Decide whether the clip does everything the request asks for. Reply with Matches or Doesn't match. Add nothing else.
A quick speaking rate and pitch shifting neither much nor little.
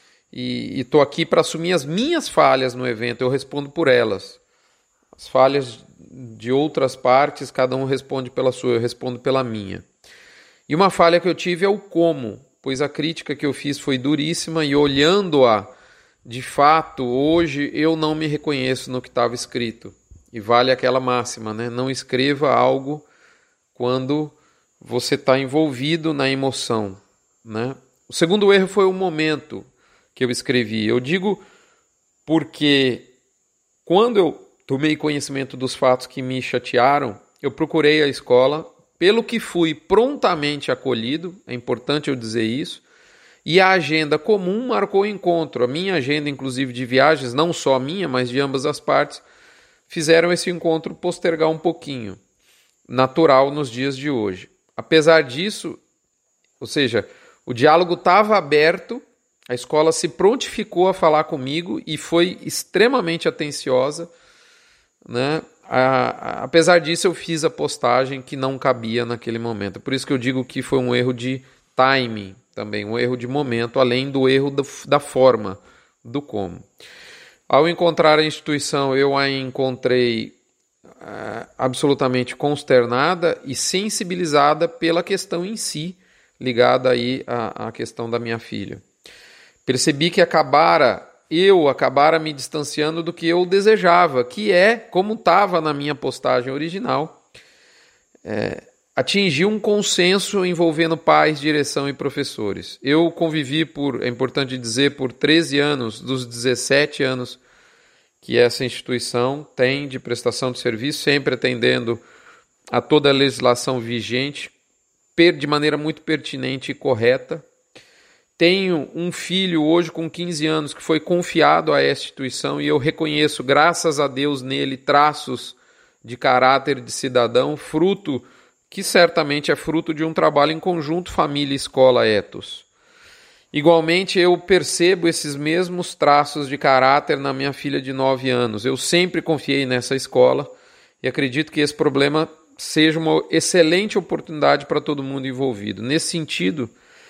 Doesn't match